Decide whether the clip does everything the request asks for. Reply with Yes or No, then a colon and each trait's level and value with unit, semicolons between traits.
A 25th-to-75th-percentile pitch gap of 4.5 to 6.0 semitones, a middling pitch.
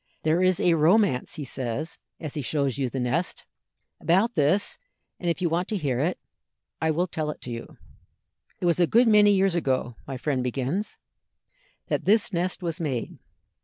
Yes: average, 5.2 semitones; medium, 160 Hz